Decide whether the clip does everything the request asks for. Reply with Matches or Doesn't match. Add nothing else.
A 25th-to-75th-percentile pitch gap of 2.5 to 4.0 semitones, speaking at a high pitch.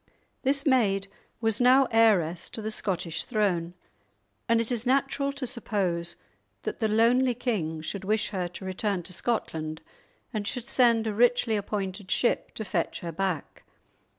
Doesn't match